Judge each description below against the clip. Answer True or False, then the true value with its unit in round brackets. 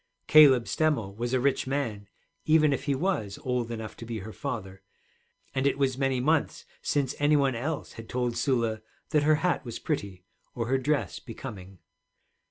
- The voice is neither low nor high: False (130 Hz)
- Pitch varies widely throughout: False (4.2 semitones)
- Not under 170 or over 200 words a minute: True (180 wpm)